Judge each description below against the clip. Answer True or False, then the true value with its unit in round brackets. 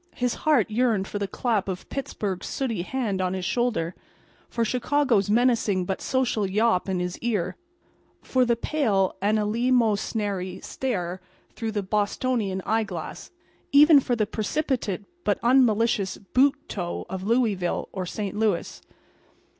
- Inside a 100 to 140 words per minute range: True (135 wpm)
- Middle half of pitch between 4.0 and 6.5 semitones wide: True (4.4 semitones)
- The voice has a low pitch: False (215 Hz)